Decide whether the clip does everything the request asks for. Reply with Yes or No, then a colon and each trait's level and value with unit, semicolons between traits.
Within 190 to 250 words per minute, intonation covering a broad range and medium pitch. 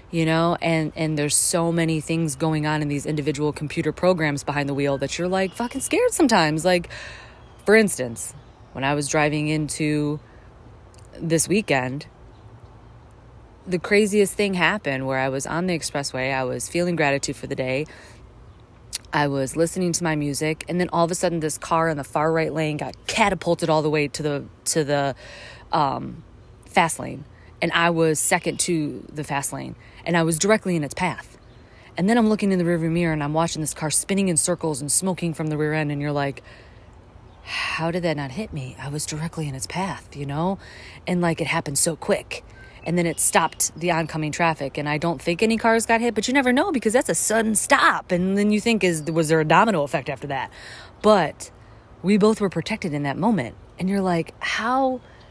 No: fast, 205 wpm; average, 4.1 semitones; medium, 155 Hz